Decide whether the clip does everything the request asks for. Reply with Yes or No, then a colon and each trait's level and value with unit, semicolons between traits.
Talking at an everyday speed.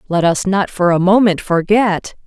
Yes: average, 185 wpm